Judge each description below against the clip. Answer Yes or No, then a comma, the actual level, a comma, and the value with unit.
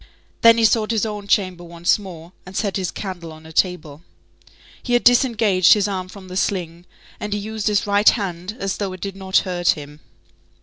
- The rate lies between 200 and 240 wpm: Yes, fast, 205 wpm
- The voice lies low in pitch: No, high, 190 Hz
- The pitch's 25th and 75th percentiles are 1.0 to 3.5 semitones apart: Yes, average, 3.0 semitones